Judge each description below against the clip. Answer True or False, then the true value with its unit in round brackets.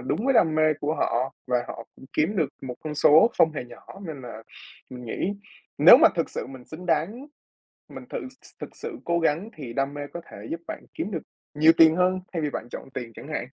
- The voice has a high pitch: False (155 Hz)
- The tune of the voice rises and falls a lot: False (4.5 semitones)